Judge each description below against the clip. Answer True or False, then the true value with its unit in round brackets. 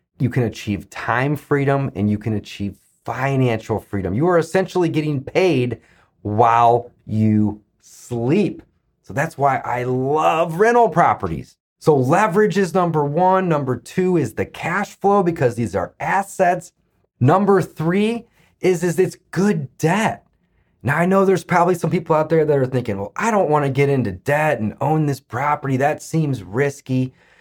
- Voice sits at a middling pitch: True (145 Hz)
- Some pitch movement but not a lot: False (6.7 semitones)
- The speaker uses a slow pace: False (165 wpm)